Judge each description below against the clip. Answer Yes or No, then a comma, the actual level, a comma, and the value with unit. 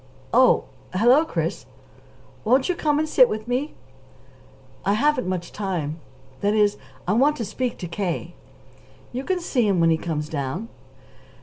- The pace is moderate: Yes, average, 160 wpm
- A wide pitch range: Yes, wide, 6.8 semitones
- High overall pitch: Yes, high, 215 Hz